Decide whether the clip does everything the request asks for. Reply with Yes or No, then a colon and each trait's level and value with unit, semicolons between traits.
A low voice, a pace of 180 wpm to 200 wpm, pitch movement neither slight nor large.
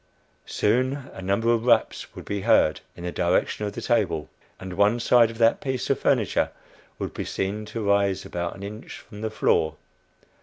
Yes: low, 105 Hz; average, 190 wpm; average, 3.4 semitones